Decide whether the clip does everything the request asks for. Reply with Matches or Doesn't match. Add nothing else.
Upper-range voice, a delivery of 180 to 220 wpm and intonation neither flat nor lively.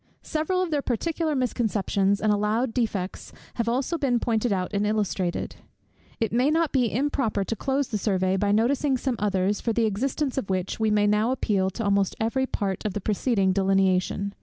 Matches